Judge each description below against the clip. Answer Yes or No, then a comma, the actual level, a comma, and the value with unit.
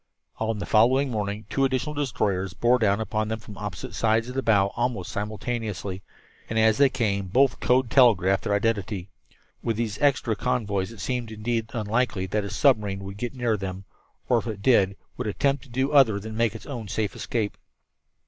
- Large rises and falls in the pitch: No, average, 3.3 semitones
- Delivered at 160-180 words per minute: No, average, 190 wpm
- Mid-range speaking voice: No, low, 110 Hz